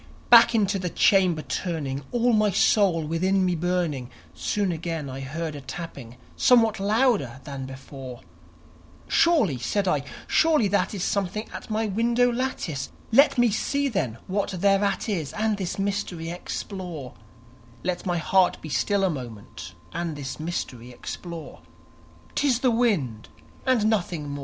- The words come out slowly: No, average, 150 wpm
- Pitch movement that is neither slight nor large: No, wide, 6.5 semitones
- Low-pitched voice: No, medium, 180 Hz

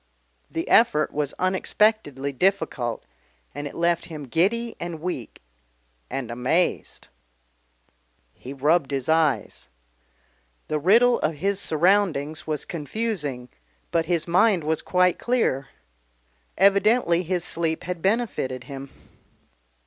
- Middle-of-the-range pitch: Yes, medium, 165 Hz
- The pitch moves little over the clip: No, average, 5.0 semitones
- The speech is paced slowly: Yes, slow, 110 wpm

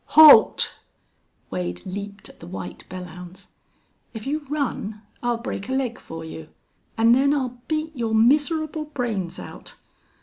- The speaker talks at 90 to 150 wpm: Yes, average, 140 wpm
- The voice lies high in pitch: Yes, high, 230 Hz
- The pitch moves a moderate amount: No, wide, 7.3 semitones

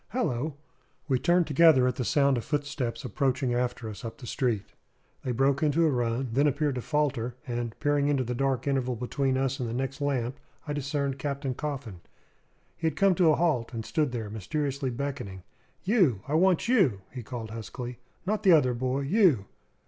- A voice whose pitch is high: No, low, 135 Hz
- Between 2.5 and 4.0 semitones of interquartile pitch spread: Yes, average, 3.3 semitones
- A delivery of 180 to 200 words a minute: Yes, average, 190 wpm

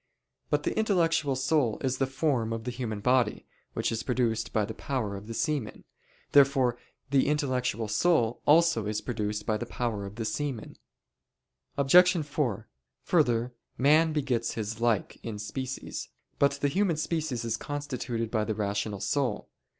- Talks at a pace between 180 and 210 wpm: No, average, 160 wpm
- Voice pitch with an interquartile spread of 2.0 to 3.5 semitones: No, average, 4.5 semitones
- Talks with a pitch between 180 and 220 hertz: No, low, 125 Hz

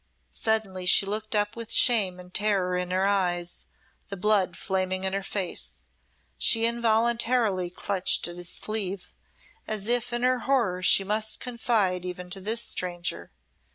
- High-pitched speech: Yes, high, 200 Hz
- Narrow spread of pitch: No, average, 3.4 semitones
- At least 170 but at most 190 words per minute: No, average, 155 wpm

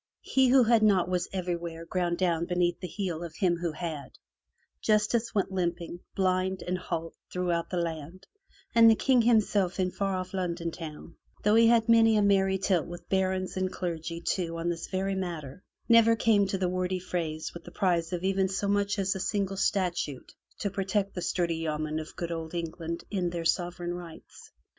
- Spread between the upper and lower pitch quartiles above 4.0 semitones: No, narrow, 2.5 semitones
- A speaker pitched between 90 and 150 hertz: No, medium, 180 Hz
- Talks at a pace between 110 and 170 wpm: No, average, 195 wpm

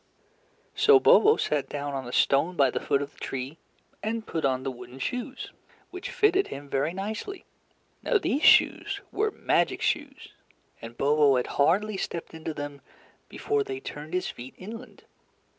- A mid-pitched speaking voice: Yes, medium, 160 Hz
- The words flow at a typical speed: Yes, average, 165 wpm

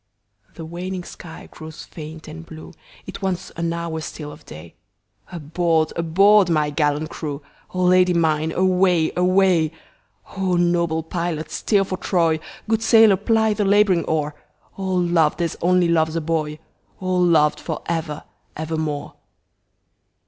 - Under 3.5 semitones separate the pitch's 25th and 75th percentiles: Yes, narrow, 2.6 semitones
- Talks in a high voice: No, medium, 170 Hz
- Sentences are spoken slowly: Yes, slow, 120 wpm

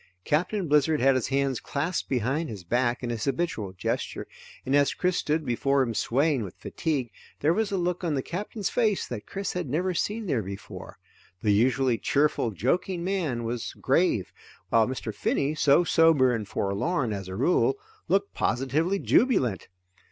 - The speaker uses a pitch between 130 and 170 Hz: Yes, medium, 140 Hz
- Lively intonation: Yes, wide, 6.5 semitones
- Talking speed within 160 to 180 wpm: Yes, average, 170 wpm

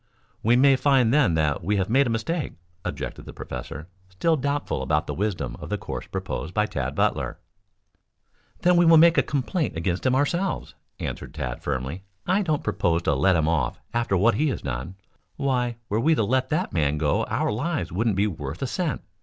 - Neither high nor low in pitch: No, low, 110 Hz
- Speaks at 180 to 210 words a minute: Yes, average, 200 wpm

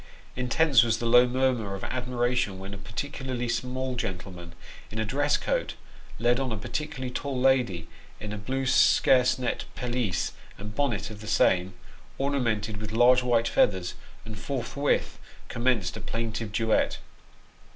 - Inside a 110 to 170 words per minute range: Yes, average, 150 wpm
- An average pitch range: Yes, average, 3.4 semitones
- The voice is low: Yes, low, 120 Hz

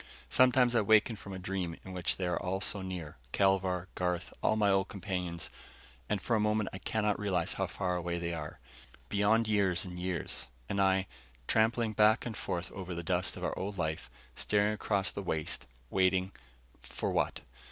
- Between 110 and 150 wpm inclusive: No, average, 185 wpm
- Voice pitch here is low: Yes, very low, 95 Hz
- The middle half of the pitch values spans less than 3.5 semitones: Yes, narrow, 2.6 semitones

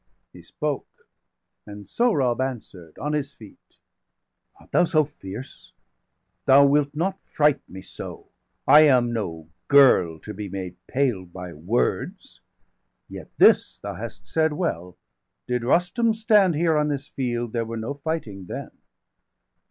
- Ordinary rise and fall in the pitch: No, wide, 6.8 semitones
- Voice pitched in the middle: No, low, 130 Hz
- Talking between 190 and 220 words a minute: No, average, 145 wpm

